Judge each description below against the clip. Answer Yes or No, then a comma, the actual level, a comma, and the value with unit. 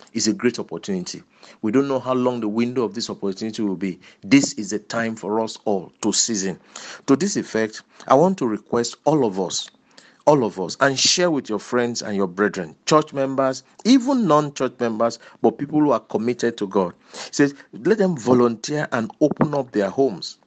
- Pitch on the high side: No, low, 125 Hz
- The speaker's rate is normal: Yes, average, 195 wpm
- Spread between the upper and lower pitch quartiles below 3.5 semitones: No, average, 4.5 semitones